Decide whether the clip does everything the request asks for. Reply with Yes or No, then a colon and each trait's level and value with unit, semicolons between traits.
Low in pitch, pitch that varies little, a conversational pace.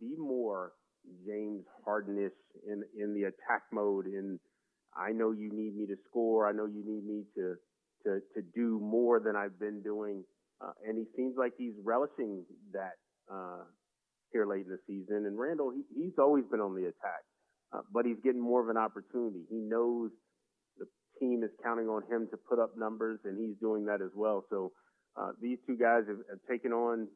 Yes: low, 110 Hz; narrow, 2.1 semitones; average, 195 wpm